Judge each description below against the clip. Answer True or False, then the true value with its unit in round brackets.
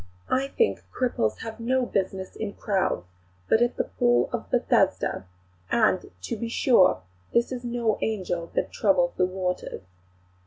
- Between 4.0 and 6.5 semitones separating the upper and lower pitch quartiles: True (5.0 semitones)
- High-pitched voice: True (220 Hz)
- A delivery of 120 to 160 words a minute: True (150 wpm)